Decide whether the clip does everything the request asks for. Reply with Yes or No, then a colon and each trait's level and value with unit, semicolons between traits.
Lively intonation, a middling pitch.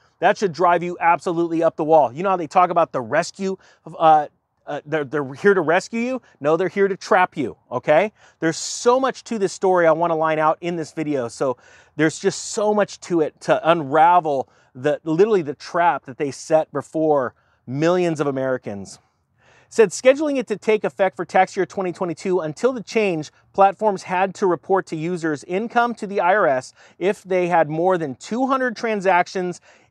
No: average, 3.9 semitones; medium, 175 Hz